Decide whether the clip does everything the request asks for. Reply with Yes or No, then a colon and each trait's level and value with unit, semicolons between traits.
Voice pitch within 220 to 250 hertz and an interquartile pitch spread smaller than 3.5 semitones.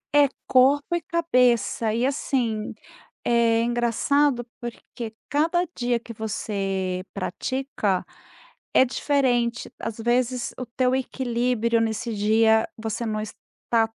Yes: high, 235 Hz; average, 2.7 semitones